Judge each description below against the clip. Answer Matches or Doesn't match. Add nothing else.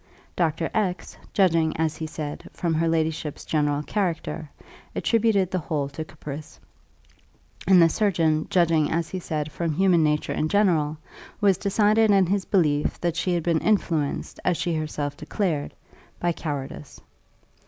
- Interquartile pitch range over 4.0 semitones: Doesn't match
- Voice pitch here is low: Doesn't match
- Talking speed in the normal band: Matches